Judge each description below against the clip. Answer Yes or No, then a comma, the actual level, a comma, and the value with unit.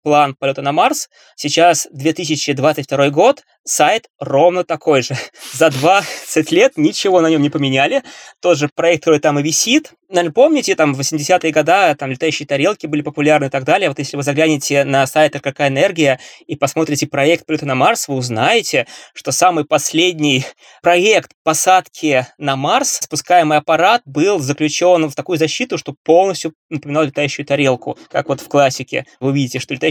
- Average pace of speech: No, fast, 165 wpm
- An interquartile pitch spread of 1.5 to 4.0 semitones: Yes, average, 3.3 semitones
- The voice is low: No, medium, 155 Hz